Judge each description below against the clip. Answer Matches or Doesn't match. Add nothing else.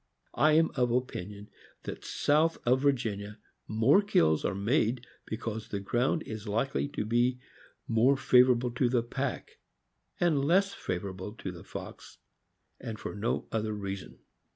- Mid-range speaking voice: Doesn't match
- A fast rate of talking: Doesn't match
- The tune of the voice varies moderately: Matches